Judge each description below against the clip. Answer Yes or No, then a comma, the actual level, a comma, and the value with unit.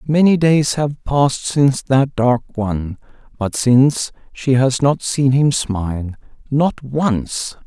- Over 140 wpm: No, slow, 135 wpm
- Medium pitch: No, low, 130 Hz